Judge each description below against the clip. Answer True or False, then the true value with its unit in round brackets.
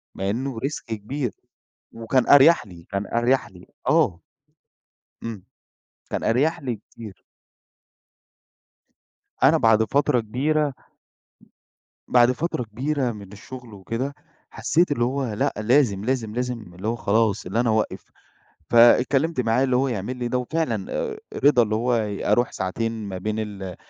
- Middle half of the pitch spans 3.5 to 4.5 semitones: True (3.9 semitones)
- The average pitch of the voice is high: False (120 Hz)